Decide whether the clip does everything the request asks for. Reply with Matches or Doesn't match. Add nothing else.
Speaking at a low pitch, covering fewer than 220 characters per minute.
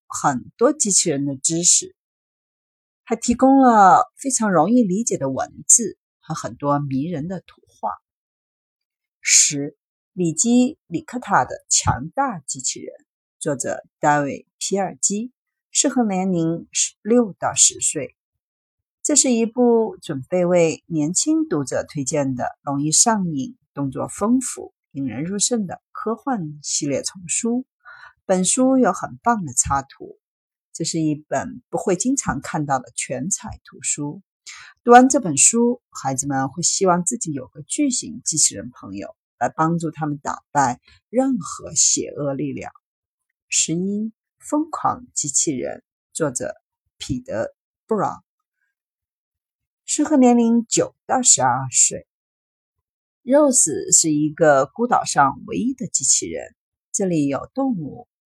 Doesn't match